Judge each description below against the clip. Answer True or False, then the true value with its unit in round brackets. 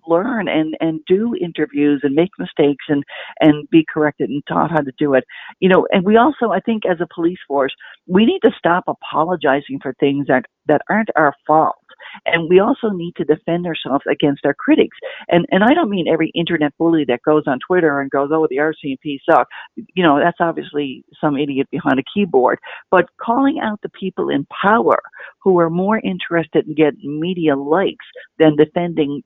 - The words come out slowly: False (195 wpm)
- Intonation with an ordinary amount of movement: True (4.0 semitones)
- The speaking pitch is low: False (160 Hz)